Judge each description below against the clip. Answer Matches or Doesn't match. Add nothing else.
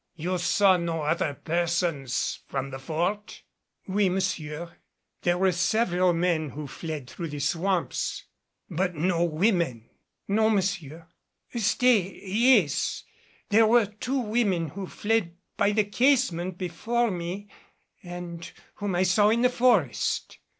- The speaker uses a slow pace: Matches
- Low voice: Doesn't match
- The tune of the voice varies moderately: Matches